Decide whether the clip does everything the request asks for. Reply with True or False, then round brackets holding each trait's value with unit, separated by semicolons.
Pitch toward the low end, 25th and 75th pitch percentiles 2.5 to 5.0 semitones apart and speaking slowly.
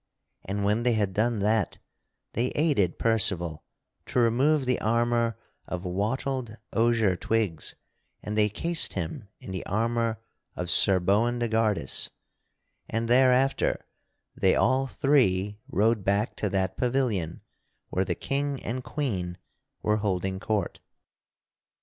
True (110 Hz; 3.9 semitones; 125 wpm)